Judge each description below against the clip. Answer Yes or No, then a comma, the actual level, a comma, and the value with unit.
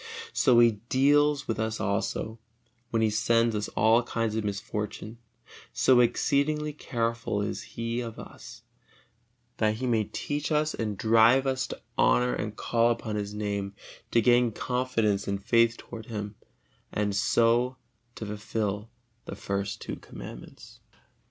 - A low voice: Yes, low, 115 Hz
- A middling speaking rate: Yes, average, 145 wpm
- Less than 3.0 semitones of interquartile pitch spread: Yes, narrow, 2.6 semitones